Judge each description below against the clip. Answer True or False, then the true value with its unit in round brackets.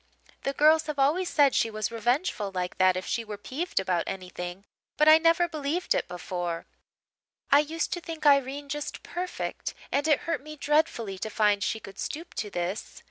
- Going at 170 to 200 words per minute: True (190 wpm)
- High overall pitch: True (275 Hz)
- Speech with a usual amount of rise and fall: False (7.6 semitones)